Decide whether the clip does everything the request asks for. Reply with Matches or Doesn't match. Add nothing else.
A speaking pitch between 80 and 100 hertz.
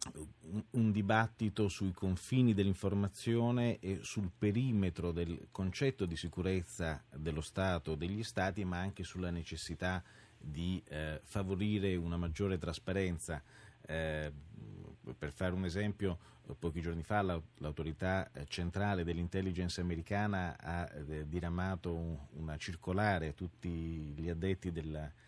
Matches